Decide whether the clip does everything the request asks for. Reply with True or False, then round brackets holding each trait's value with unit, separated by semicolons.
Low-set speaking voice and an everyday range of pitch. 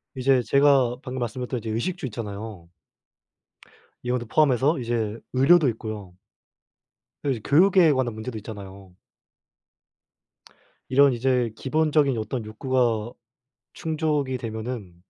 True (125 Hz; 3.9 semitones)